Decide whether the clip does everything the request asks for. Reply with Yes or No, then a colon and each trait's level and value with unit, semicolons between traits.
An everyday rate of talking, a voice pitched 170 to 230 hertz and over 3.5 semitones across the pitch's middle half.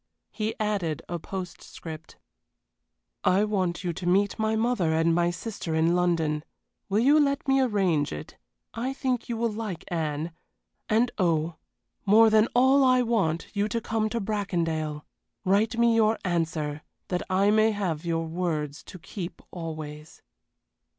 Yes: average, 150 wpm; medium, 185 Hz; average, 5.1 semitones